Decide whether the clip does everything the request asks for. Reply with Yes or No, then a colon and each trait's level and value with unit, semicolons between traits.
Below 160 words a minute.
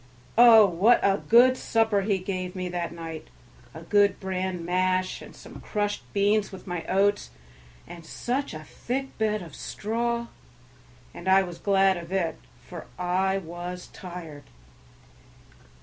Yes: average, 145 wpm